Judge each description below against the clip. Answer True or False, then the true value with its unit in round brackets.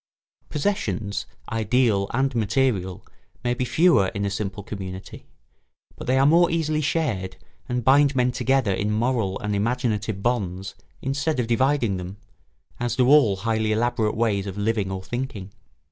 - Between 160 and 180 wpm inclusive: False (150 wpm)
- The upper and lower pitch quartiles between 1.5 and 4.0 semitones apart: False (4.7 semitones)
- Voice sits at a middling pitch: False (115 Hz)